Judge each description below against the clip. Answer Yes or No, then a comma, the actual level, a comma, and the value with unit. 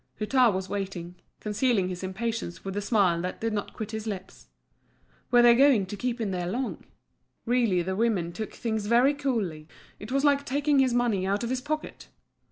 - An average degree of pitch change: Yes, average, 4.5 semitones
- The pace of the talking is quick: No, average, 190 wpm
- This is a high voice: Yes, high, 220 Hz